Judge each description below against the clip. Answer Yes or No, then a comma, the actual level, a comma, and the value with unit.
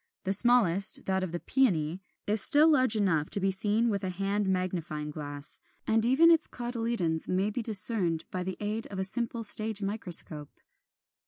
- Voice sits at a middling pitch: No, high, 200 Hz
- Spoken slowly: No, average, 175 wpm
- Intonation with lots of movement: No, average, 4.0 semitones